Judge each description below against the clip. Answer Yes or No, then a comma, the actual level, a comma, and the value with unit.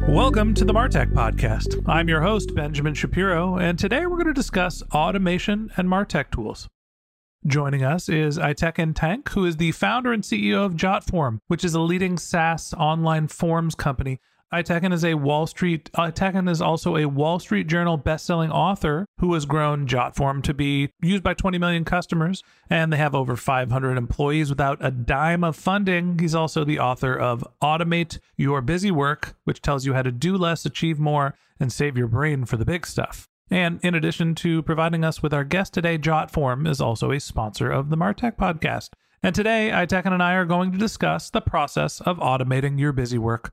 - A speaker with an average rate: Yes, average, 190 wpm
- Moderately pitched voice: Yes, medium, 160 Hz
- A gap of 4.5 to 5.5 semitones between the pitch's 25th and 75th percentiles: No, average, 4.0 semitones